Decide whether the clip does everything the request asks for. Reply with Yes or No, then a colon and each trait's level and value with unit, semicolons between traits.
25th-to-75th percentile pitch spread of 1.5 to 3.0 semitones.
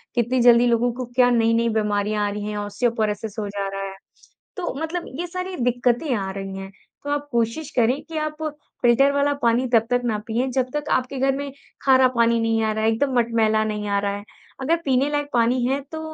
No: average, 3.8 semitones